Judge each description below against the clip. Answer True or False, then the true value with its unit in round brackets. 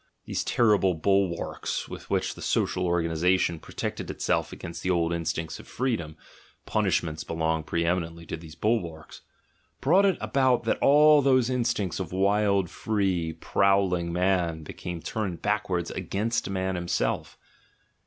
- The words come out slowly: False (145 wpm)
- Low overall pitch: True (90 Hz)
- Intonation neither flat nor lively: True (4.1 semitones)